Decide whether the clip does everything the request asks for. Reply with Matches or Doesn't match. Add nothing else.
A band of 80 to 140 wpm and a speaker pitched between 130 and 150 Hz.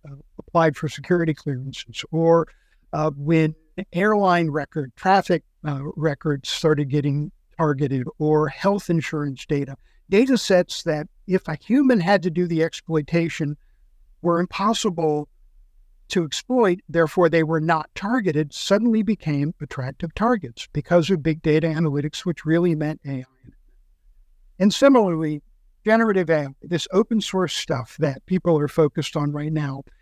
Doesn't match